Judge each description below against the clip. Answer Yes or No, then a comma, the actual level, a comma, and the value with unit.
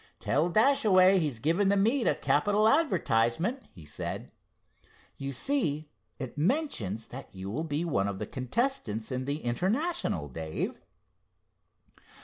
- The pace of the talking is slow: Yes, slow, 130 wpm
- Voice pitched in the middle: Yes, medium, 155 Hz